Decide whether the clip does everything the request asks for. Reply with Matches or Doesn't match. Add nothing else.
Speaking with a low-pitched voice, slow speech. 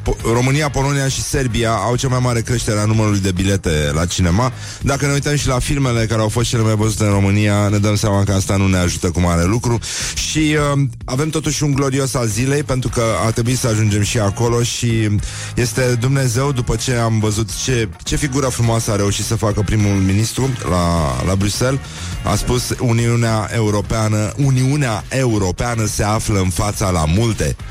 Doesn't match